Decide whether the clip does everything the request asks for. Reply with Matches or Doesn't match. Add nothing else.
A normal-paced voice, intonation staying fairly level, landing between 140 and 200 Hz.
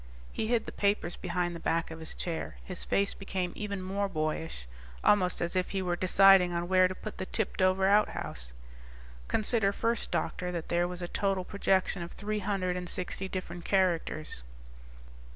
Matches